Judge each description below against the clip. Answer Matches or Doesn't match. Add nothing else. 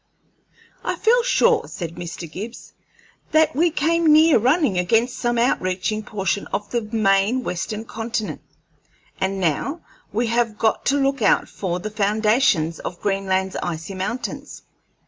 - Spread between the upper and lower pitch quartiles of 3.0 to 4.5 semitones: Doesn't match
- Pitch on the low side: Doesn't match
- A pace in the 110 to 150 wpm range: Matches